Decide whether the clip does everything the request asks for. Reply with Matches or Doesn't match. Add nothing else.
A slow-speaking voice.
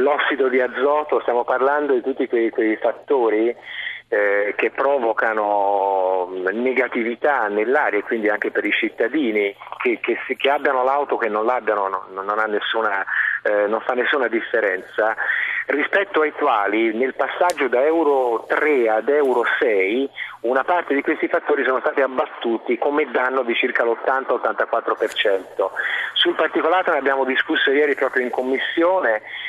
Doesn't match